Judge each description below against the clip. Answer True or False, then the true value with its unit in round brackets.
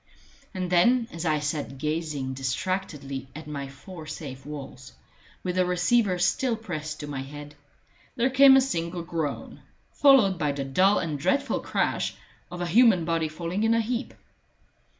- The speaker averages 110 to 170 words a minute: True (160 wpm)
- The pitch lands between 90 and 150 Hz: False (170 Hz)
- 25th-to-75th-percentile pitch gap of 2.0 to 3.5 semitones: False (4.9 semitones)